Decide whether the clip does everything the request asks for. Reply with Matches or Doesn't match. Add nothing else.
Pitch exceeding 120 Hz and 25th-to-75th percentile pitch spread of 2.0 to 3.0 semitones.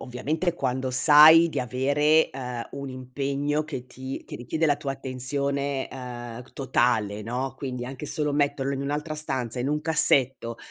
Matches